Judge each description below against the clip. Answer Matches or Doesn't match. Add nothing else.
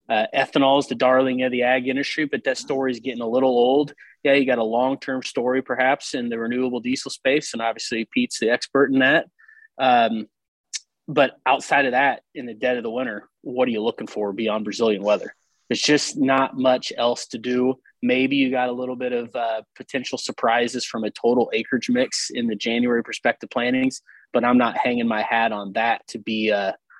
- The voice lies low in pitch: Matches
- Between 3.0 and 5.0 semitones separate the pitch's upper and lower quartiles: Doesn't match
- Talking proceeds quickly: Matches